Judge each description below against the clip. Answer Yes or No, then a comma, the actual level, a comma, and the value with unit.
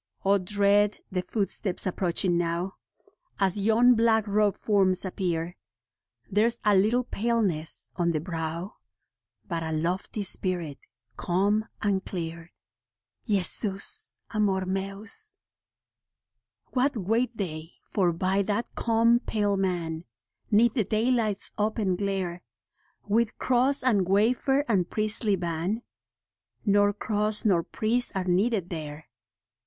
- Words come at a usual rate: No, slow, 115 wpm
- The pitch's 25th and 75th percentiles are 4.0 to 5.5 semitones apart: No, average, 3.5 semitones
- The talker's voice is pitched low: No, high, 200 Hz